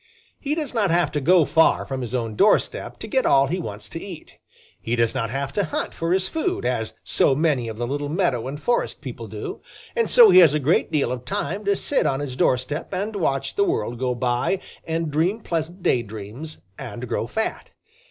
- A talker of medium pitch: Yes, medium, 150 Hz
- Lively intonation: Yes, wide, 7.0 semitones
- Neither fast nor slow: No, fast, 215 wpm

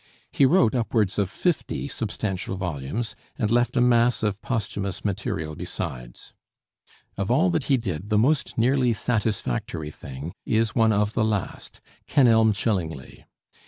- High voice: No, low, 110 Hz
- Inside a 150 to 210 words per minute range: No, average, 140 wpm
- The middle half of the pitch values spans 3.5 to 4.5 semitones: Yes, average, 4.1 semitones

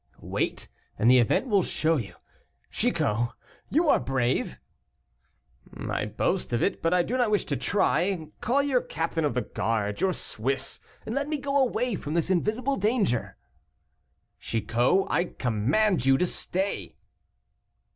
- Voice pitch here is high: No, medium, 175 Hz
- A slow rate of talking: No, average, 150 wpm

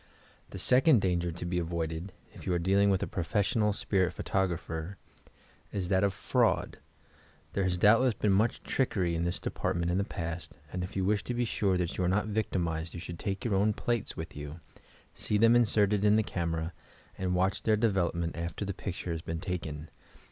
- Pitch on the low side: Yes, very low, 95 Hz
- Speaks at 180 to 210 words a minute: Yes, average, 200 wpm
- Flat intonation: No, average, 3.3 semitones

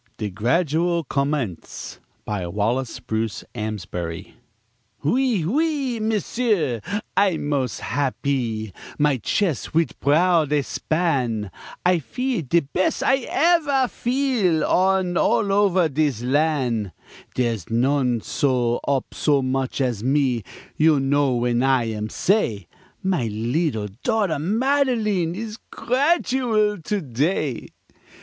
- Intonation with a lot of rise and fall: Yes, wide, 8.3 semitones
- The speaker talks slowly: Yes, slow, 115 wpm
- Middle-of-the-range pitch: Yes, medium, 145 Hz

